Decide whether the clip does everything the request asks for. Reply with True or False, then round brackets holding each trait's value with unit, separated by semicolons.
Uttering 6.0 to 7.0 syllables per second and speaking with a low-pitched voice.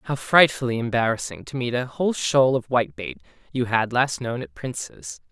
False (5.2 syllables/s; 120 Hz)